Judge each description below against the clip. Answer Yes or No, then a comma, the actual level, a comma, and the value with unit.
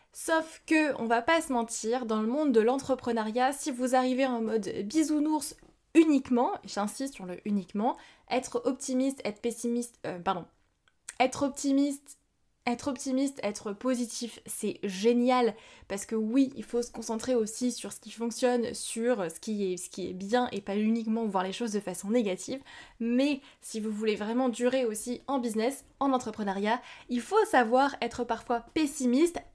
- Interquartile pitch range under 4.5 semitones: Yes, average, 3.2 semitones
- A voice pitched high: Yes, high, 240 Hz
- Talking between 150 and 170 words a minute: Yes, average, 165 wpm